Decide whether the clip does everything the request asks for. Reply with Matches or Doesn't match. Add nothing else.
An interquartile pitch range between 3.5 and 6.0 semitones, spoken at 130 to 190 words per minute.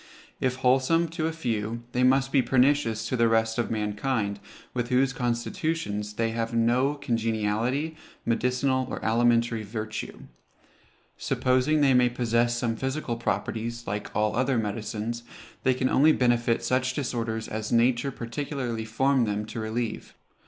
Doesn't match